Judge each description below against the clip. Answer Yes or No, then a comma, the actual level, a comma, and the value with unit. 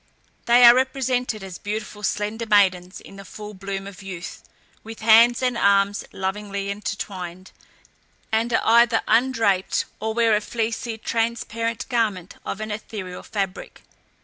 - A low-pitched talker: No, high, 215 Hz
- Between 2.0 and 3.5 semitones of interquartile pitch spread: Yes, average, 2.7 semitones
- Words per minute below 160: Yes, average, 140 wpm